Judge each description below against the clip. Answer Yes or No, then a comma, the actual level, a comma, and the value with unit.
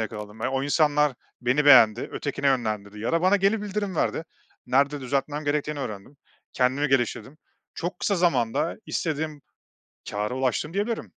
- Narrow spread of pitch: No, average, 4.4 semitones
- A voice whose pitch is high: No, medium, 140 Hz